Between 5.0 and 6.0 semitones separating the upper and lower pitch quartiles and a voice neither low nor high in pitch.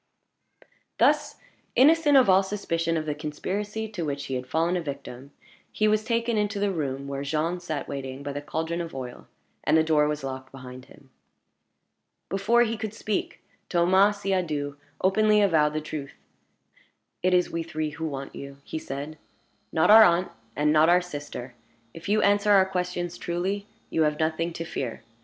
Yes: average, 5.3 semitones; medium, 165 Hz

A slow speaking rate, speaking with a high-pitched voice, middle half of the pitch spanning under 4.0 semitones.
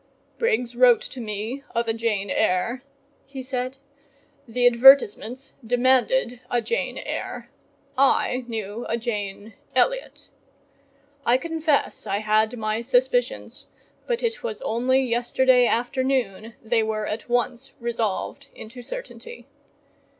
Yes: slow, 115 wpm; high, 245 Hz; average, 3.5 semitones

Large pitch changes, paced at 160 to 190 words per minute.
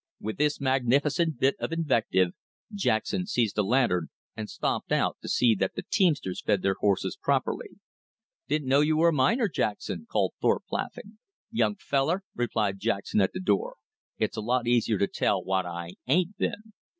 Yes: wide, 8.1 semitones; average, 175 wpm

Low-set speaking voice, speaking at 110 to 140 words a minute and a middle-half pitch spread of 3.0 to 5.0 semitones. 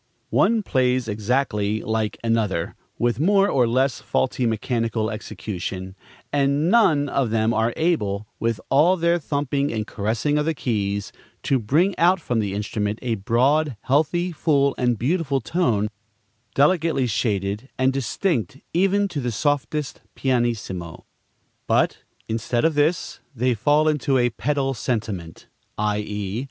No: low, 125 Hz; slow, 135 wpm; wide, 5.4 semitones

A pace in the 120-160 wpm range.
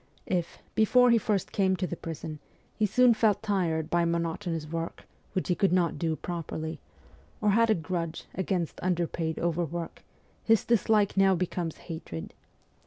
Yes: average, 155 wpm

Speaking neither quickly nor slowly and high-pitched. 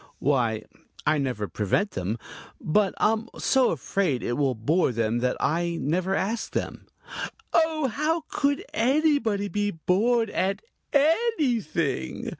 No: slow, 125 wpm; high, 195 Hz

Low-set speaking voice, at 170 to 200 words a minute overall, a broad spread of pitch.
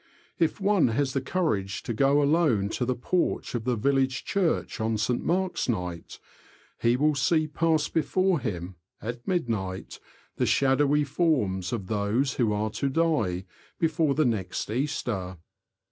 No: low, 130 Hz; average, 150 wpm; wide, 6.4 semitones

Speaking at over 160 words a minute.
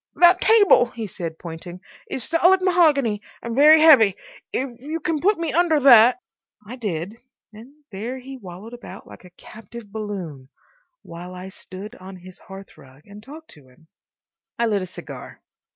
Yes: average, 170 wpm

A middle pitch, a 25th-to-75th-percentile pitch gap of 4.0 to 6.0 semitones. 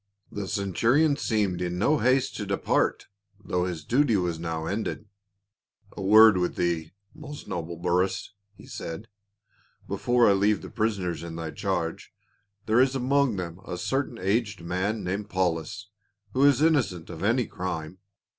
No: low, 100 Hz; average, 5.1 semitones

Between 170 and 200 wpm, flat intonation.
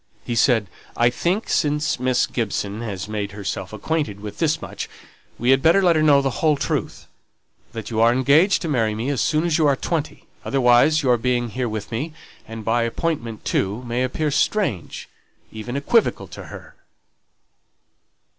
No: average, 175 wpm; wide, 5.4 semitones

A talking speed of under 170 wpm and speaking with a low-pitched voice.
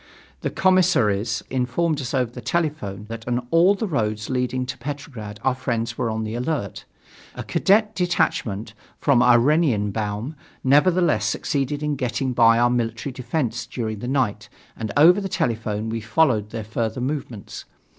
Yes: average, 155 wpm; low, 125 Hz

